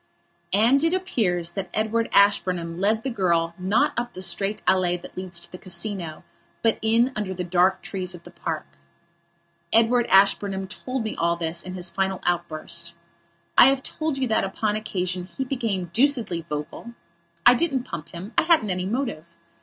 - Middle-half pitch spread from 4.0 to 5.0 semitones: Yes, average, 4.6 semitones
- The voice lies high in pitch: Yes, high, 195 Hz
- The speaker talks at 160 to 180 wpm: Yes, average, 175 wpm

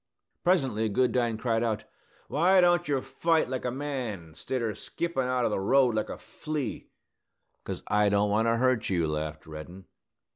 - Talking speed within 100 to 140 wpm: No, average, 170 wpm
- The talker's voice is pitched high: No, low, 115 Hz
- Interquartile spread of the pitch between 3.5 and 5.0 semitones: Yes, average, 4.7 semitones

